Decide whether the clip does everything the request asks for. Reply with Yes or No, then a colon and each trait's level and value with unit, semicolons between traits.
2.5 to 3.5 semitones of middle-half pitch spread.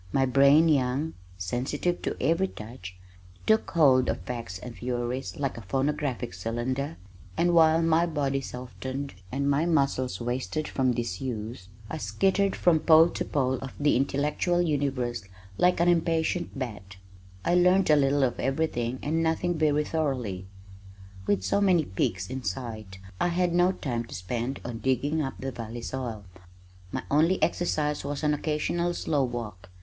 No: average, 4.9 semitones